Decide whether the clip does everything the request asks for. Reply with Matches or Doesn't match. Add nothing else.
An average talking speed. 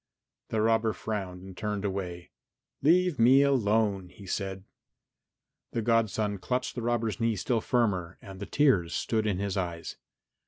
Matches